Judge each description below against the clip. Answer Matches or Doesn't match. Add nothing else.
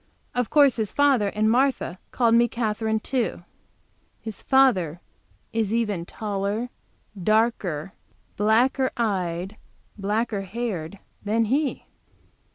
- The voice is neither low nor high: Doesn't match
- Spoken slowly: Matches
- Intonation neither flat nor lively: Matches